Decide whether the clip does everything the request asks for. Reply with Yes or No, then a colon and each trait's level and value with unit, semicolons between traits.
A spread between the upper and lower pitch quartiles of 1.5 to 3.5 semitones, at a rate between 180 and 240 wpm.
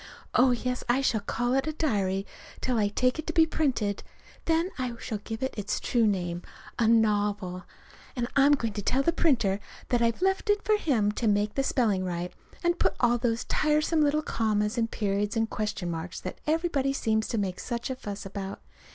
No: average, 4.9 semitones; fast, 205 wpm